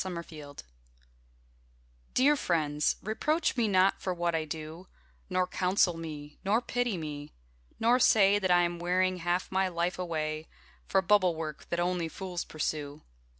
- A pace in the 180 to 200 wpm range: No, average, 150 wpm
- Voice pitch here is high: No, medium, 175 Hz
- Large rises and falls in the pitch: No, average, 3.2 semitones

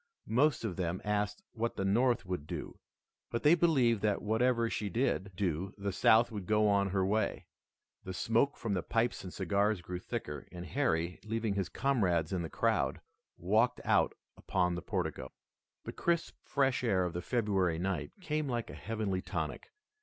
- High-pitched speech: No, low, 100 Hz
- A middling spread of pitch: Yes, average, 4.4 semitones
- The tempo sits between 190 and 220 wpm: No, average, 175 wpm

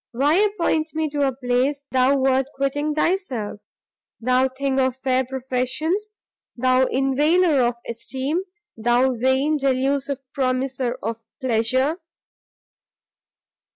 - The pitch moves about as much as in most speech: No, narrow, 2.3 semitones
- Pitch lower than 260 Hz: No, very high, 265 Hz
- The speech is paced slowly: Yes, slow, 110 wpm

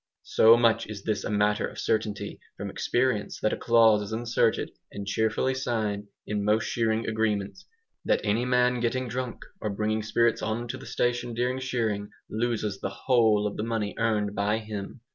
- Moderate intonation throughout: No, narrow, 2.3 semitones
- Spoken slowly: No, average, 180 wpm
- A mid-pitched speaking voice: No, low, 110 Hz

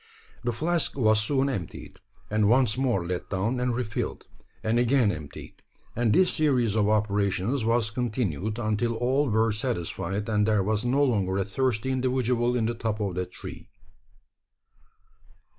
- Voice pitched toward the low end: Yes, low, 115 Hz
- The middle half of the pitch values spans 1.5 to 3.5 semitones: Yes, average, 3.2 semitones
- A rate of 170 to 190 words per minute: No, average, 160 wpm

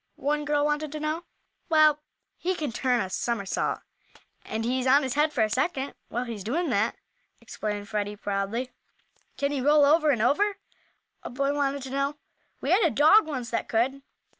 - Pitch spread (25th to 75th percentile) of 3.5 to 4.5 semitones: Yes, average, 4.2 semitones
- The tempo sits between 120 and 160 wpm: No, average, 185 wpm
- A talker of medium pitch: No, very high, 275 Hz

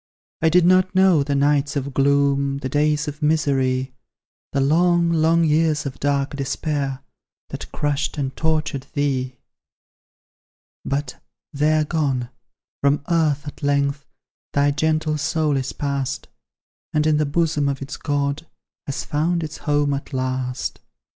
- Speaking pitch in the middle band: Yes, medium, 145 Hz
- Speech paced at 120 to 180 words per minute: Yes, average, 140 wpm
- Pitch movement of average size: No, narrow, 2.0 semitones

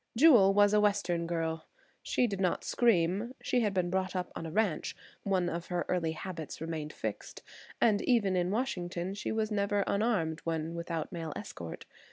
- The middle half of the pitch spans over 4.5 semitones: No, average, 3.7 semitones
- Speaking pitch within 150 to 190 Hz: Yes, medium, 185 Hz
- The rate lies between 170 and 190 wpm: Yes, average, 180 wpm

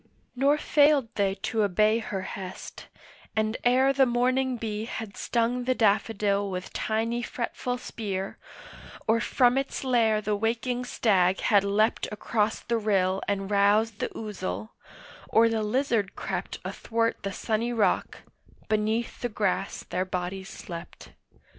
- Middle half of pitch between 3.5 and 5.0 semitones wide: No, average, 3.1 semitones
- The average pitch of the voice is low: No, high, 220 Hz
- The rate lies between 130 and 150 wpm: Yes, average, 140 wpm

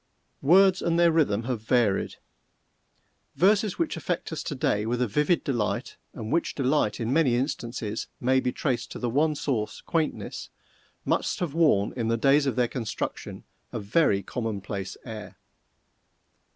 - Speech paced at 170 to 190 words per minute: No, average, 155 wpm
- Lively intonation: Yes, wide, 5.8 semitones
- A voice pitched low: Yes, low, 125 Hz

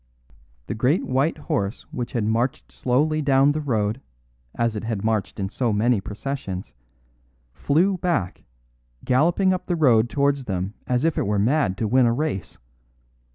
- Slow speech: No, average, 160 wpm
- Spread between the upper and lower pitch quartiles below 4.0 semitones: No, wide, 5.4 semitones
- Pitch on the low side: Yes, low, 125 Hz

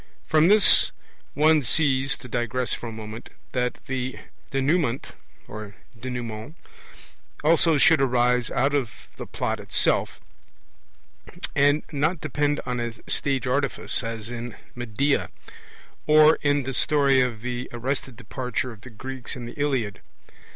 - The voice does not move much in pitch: No, average, 3.2 semitones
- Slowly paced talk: Yes, slow, 130 wpm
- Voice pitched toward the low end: Yes, low, 130 Hz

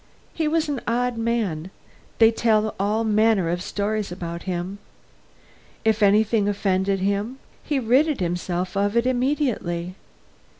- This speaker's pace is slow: Yes, slow, 130 wpm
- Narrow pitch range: No, average, 3.9 semitones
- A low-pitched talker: No, high, 210 Hz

